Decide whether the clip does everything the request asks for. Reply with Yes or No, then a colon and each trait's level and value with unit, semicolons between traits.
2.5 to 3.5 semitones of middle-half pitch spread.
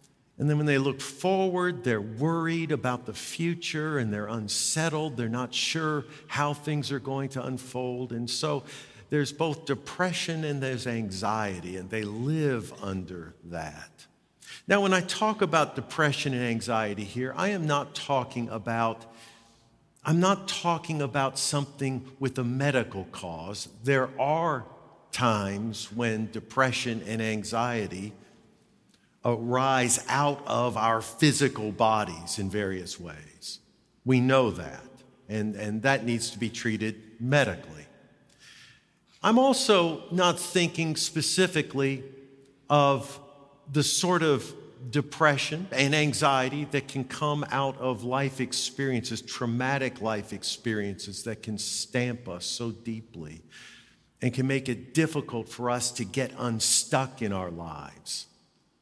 No: average, 4.4 semitones